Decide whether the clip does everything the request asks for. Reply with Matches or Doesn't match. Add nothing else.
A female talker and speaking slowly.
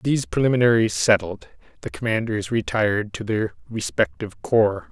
Doesn't match